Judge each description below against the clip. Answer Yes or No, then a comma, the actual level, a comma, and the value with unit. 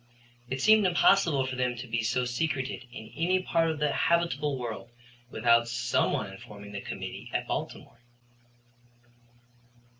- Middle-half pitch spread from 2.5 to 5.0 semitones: No, wide, 5.6 semitones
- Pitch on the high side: No, low, 125 Hz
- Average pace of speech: Yes, average, 145 wpm